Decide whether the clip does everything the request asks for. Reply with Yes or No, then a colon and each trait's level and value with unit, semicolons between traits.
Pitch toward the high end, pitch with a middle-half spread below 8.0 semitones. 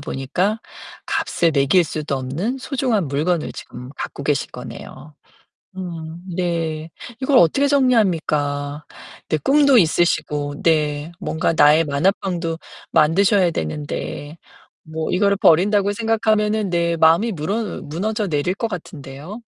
No: medium, 170 Hz; average, 5.3 semitones